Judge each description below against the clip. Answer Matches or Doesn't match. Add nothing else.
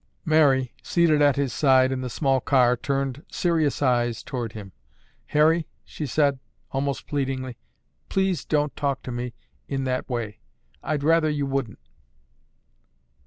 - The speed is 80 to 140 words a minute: Matches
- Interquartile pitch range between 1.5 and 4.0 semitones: Matches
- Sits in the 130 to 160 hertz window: Matches